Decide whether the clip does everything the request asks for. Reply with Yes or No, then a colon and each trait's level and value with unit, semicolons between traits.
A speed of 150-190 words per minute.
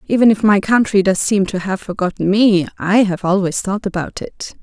No: fast, 205 wpm